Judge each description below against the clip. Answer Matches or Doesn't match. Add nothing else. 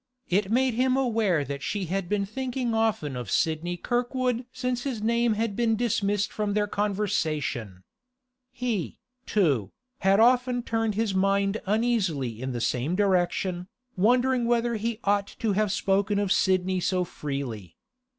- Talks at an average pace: Matches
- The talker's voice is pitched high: Matches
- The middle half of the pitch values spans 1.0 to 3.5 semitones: Doesn't match